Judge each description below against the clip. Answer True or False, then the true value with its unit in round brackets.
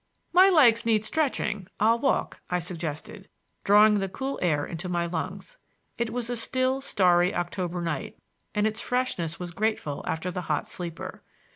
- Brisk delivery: False (160 wpm)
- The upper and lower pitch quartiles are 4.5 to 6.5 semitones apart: True (5.0 semitones)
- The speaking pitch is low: False (195 Hz)